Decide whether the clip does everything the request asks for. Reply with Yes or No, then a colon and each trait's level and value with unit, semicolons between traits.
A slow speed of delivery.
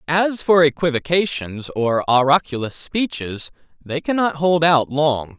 Yes: slow, 125 wpm